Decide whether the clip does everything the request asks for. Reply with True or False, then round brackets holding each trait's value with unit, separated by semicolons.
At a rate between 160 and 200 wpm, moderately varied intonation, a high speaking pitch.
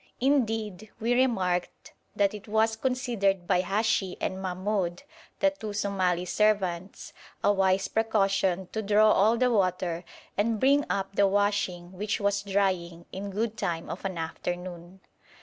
False (145 wpm; 3.0 semitones; 200 Hz)